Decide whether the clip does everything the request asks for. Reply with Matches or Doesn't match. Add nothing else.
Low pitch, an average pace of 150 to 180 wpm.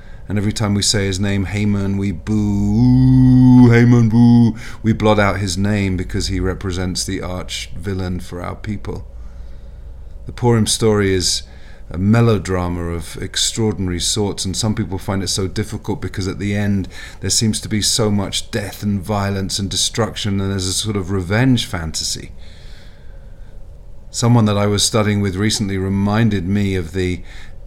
Matches